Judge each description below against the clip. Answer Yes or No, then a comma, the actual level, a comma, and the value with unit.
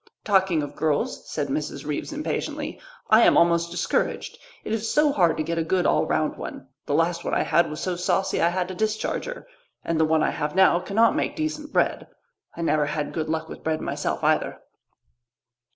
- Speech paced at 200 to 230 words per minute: Yes, fast, 205 wpm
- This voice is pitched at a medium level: Yes, medium, 170 Hz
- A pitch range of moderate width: Yes, average, 4.2 semitones